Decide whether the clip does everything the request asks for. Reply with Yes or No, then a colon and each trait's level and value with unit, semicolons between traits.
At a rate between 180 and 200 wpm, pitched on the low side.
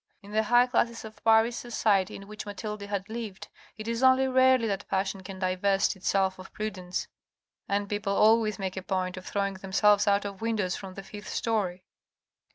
No: average, 185 wpm; high, 205 Hz